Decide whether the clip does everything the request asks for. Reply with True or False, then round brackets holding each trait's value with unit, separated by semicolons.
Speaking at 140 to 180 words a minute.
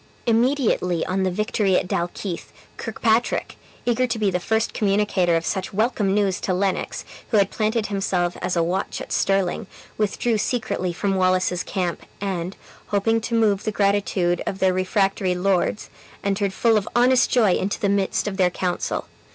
True (170 wpm)